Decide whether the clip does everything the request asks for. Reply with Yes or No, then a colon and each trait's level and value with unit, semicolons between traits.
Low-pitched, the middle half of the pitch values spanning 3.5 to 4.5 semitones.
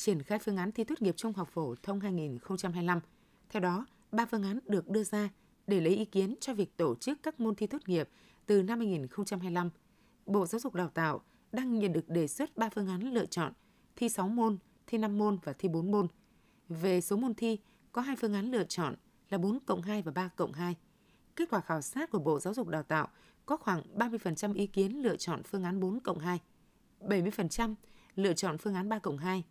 No: high, 200 Hz; average, 3.8 semitones